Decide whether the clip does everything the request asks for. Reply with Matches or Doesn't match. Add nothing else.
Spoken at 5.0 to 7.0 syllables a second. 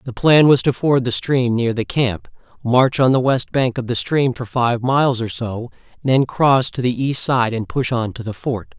Doesn't match